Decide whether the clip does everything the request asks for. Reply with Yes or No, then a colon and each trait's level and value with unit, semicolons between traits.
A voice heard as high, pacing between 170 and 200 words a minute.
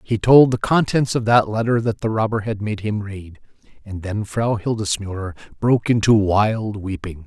No: low, 105 Hz; average, 180 wpm